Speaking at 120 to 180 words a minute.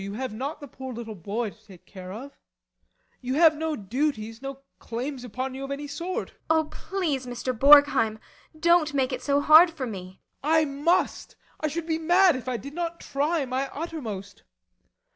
No: average, 195 wpm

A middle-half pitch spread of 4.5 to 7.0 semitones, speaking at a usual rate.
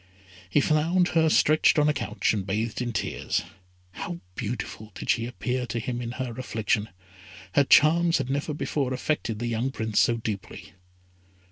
Yes: average, 4.9 semitones; average, 165 wpm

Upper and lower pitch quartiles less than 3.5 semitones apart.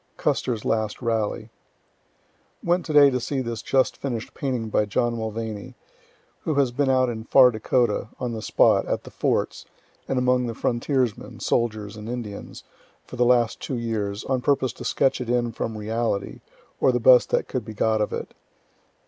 Yes: narrow, 2.6 semitones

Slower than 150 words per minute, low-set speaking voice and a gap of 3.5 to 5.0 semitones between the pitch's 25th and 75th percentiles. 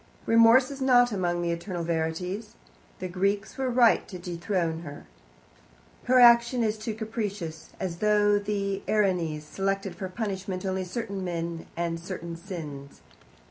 No: average, 140 wpm; high, 190 Hz; average, 4.0 semitones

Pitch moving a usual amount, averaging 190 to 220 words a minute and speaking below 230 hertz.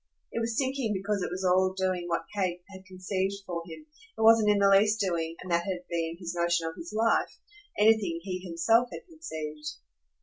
Yes: average, 3.5 semitones; average, 200 wpm; medium, 185 Hz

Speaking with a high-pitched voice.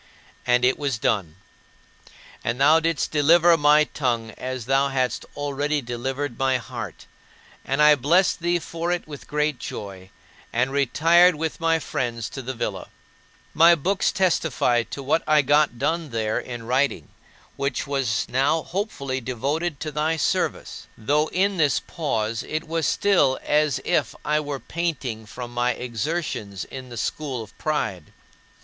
No: medium, 140 Hz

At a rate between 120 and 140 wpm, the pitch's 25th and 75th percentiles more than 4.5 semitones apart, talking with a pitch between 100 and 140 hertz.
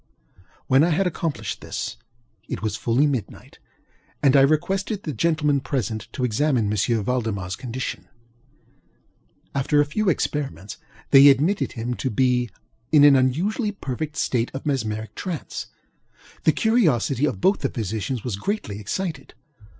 Yes: slow, 135 wpm; average, 5.2 semitones; low, 135 Hz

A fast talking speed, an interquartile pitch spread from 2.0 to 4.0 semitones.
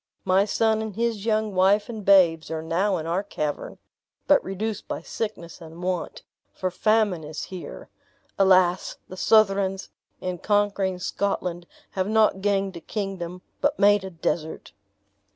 No: average, 150 wpm; narrow, 2.6 semitones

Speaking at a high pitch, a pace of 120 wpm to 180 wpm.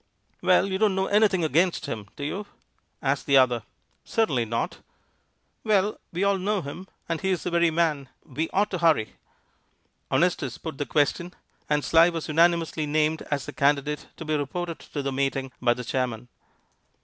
No: medium, 155 Hz; average, 175 wpm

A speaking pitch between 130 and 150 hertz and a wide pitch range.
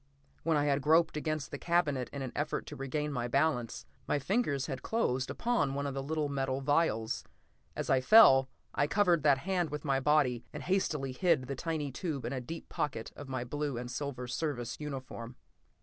No: medium, 140 Hz; average, 2.9 semitones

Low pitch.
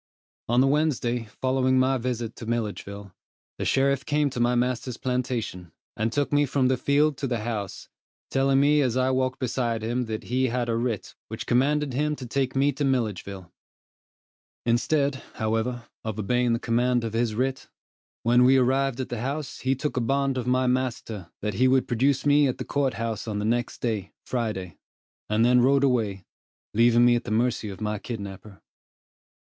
Yes: low, 125 Hz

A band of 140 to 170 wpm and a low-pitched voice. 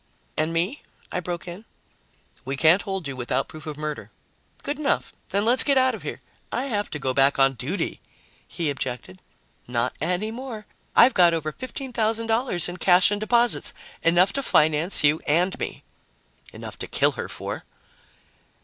No: average, 165 wpm; medium, 175 Hz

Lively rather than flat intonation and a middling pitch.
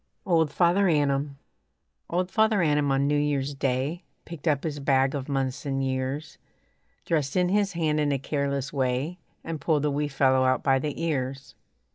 No: average, 3.0 semitones; medium, 145 Hz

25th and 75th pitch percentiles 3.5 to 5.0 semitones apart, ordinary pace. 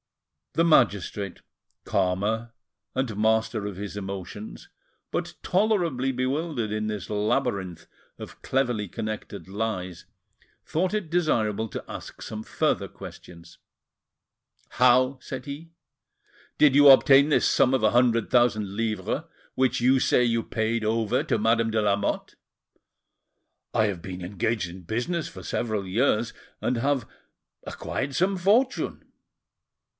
No: average, 4.4 semitones; slow, 125 wpm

